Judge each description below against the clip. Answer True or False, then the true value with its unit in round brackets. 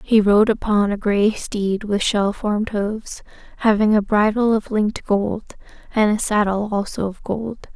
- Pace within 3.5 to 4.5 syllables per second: True (4.4 syllables/s)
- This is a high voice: True (210 Hz)